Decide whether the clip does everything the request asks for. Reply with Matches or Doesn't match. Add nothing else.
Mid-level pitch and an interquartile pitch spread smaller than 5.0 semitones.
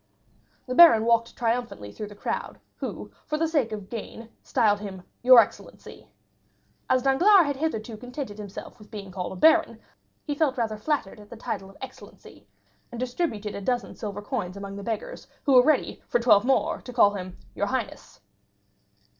Doesn't match